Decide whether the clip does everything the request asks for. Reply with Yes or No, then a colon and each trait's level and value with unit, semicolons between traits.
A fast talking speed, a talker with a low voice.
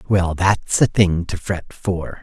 No: average, 190 wpm; very low, 90 Hz